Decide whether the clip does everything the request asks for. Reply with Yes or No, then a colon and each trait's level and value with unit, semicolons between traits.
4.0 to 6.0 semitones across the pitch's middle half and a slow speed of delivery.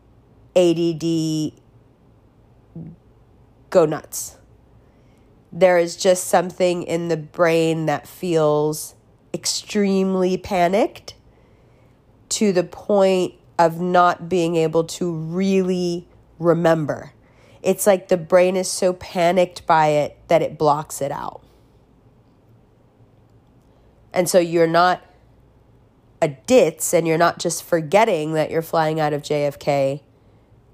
Yes: average, 5.2 semitones; slow, 105 wpm